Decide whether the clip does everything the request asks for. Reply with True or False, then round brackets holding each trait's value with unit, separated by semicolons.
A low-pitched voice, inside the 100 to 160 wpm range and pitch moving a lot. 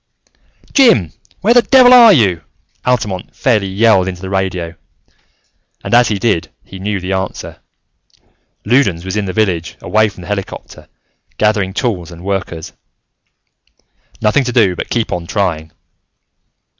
False (100 Hz; 145 wpm; 4.1 semitones)